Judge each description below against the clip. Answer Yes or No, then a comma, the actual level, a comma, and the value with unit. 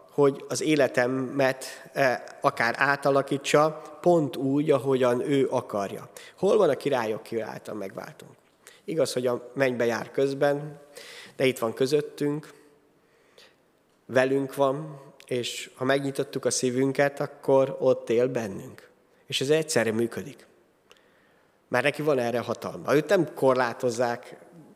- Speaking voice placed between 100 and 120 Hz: No, low, 135 Hz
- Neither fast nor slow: Yes, average, 120 wpm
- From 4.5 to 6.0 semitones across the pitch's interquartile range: No, narrow, 2.4 semitones